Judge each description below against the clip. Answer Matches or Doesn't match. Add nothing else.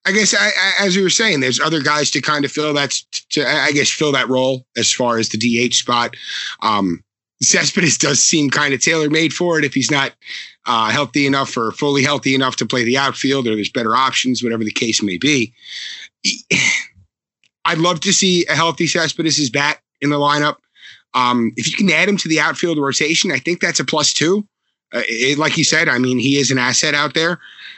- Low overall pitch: Doesn't match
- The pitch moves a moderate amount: Matches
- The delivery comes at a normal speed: Doesn't match